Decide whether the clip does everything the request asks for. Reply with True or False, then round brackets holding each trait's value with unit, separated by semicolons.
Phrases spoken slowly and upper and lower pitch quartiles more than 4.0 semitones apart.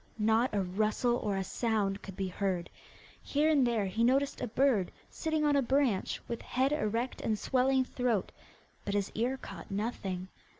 False (175 wpm; 4.8 semitones)